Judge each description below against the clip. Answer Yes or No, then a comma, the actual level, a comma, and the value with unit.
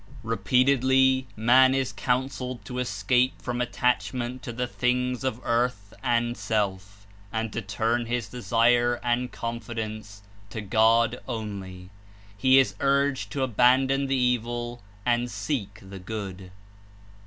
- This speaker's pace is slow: Yes, slow, 130 wpm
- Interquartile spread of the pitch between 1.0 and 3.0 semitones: Yes, narrow, 2.5 semitones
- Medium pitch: No, low, 120 Hz